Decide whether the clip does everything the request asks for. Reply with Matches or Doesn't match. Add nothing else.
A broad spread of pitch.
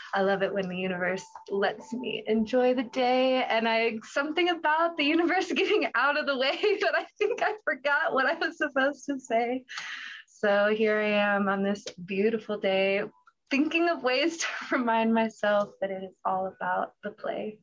Matches